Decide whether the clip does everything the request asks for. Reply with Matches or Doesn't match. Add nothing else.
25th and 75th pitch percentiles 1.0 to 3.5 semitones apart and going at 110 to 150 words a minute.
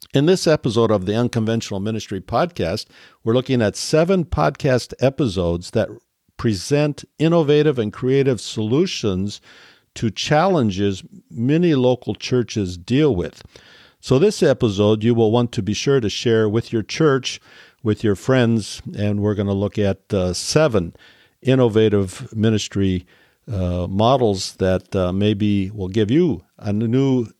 Doesn't match